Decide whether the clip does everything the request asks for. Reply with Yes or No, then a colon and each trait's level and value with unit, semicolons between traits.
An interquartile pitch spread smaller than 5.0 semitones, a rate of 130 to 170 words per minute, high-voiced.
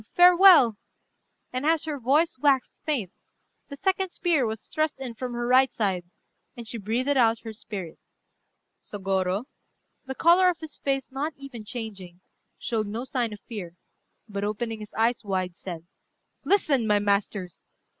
No: wide, 5.4 semitones; average, 155 wpm; high, 235 Hz